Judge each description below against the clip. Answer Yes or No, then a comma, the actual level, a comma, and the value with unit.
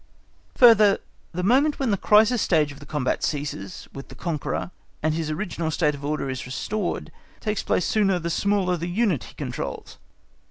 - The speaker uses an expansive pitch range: Yes, wide, 5.8 semitones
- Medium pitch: Yes, medium, 175 Hz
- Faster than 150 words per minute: Yes, average, 175 wpm